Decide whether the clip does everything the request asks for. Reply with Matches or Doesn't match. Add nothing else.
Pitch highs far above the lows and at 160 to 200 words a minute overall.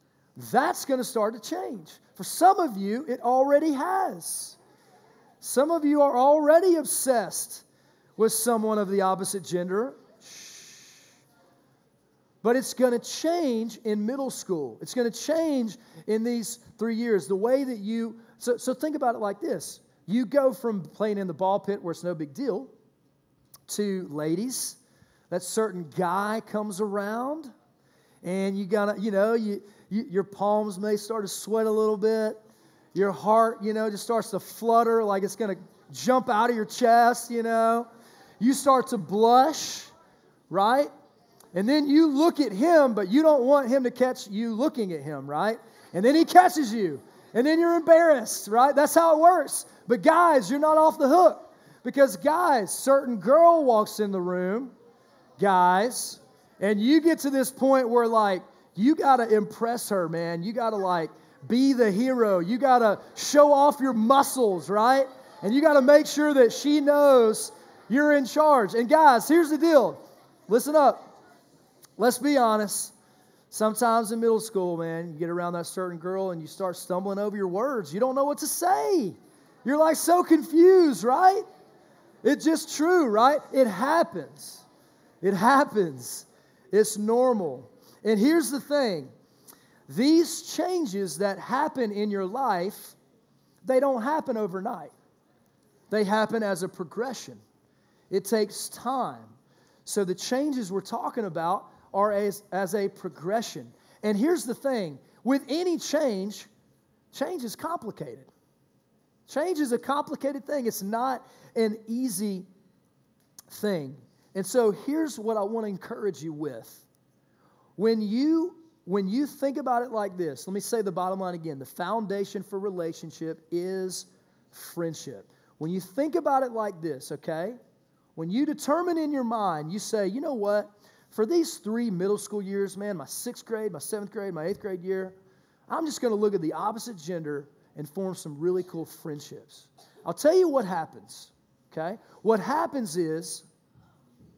Matches